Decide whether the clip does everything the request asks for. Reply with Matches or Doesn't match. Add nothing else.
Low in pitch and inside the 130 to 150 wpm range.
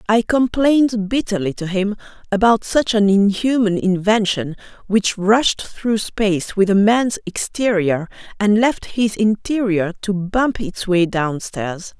Doesn't match